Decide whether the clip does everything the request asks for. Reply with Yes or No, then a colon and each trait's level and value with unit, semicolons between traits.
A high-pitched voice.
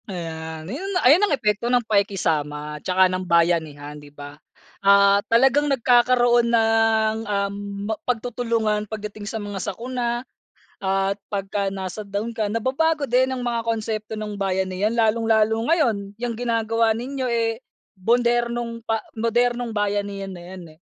Yes: high, 220 Hz